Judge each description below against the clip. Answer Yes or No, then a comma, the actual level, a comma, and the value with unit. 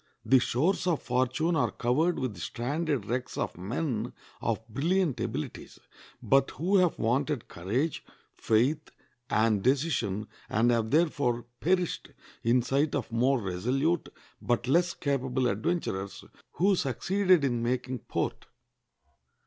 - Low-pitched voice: Yes, low, 130 Hz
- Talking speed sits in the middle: No, slow, 125 wpm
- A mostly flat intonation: No, average, 5.2 semitones